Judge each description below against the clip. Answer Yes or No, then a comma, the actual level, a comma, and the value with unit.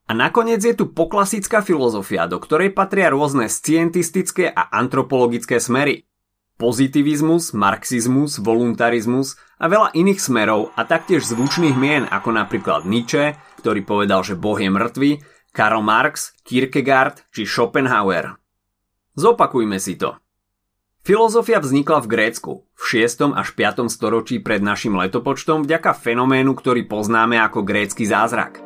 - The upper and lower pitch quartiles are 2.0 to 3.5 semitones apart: No, wide, 6.5 semitones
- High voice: No, low, 130 Hz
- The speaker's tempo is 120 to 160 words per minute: Yes, average, 130 wpm